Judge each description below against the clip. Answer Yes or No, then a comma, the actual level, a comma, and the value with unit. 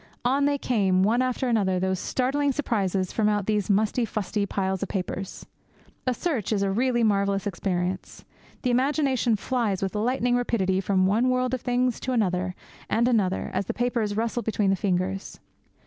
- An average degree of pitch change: Yes, average, 4.3 semitones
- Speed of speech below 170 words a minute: No, average, 175 wpm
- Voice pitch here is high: Yes, high, 215 Hz